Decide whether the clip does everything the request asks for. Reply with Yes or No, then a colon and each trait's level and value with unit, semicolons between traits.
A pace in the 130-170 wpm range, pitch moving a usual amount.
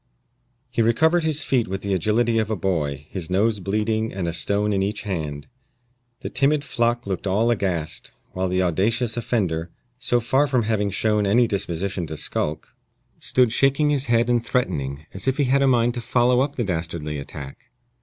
No: average, 185 wpm; average, 4.8 semitones